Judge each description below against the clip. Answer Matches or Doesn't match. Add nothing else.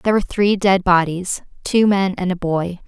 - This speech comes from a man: Doesn't match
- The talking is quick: Matches